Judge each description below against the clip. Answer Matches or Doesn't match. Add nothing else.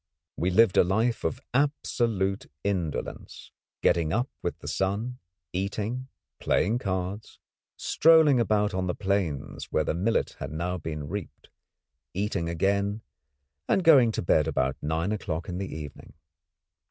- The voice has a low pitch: Matches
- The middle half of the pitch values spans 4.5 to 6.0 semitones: Matches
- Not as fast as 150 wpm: Matches